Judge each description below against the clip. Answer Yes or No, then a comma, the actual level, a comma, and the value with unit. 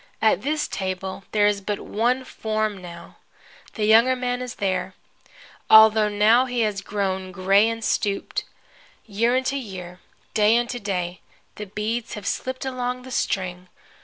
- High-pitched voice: Yes, high, 210 Hz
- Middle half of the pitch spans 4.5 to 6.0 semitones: No, average, 3.8 semitones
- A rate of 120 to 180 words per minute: Yes, average, 150 wpm